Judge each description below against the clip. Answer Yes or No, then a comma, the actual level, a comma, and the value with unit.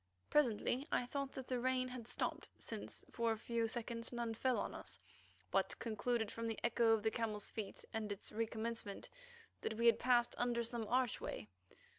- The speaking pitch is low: No, high, 235 Hz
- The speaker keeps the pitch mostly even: Yes, narrow, 1.7 semitones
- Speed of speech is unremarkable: Yes, average, 180 wpm